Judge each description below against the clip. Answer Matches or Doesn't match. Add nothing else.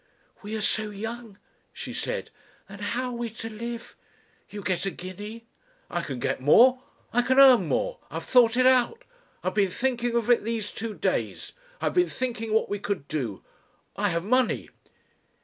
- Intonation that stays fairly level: Doesn't match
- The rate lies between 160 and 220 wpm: Matches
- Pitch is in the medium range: Doesn't match